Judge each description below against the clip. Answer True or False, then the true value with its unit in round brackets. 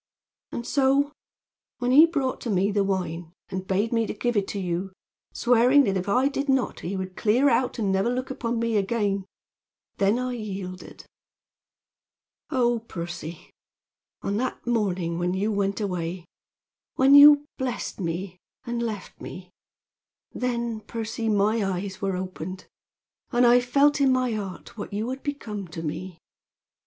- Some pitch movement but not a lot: True (4.7 semitones)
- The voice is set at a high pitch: True (215 Hz)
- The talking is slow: False (155 wpm)